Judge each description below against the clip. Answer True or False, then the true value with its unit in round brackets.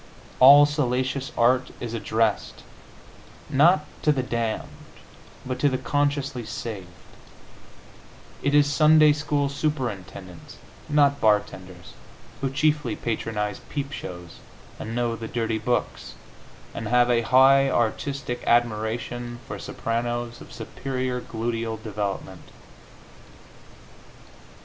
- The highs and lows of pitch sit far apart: False (3.8 semitones)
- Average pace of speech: False (105 wpm)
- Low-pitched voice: True (120 Hz)